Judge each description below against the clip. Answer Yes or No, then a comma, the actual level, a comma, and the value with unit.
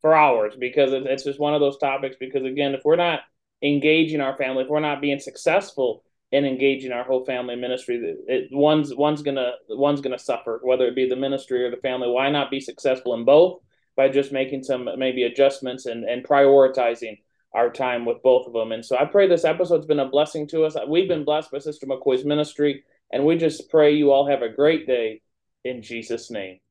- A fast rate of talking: Yes, fast, 215 wpm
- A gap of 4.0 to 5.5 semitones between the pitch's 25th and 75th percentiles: No, average, 2.7 semitones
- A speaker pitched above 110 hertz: Yes, low, 135 Hz